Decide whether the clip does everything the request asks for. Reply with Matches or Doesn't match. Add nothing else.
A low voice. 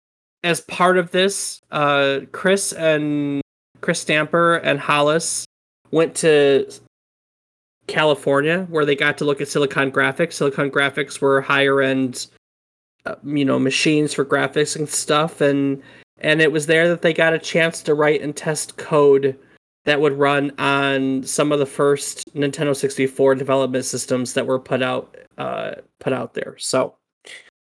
Doesn't match